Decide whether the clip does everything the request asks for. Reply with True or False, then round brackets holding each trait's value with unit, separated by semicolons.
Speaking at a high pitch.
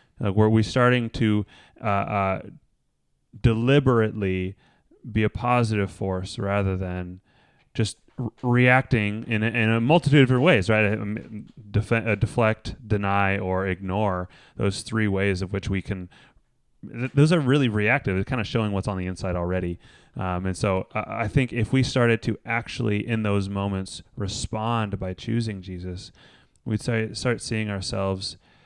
False (110 Hz)